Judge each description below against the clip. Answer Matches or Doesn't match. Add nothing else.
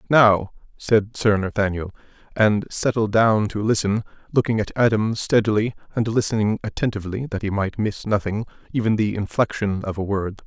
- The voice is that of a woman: Doesn't match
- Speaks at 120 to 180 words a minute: Matches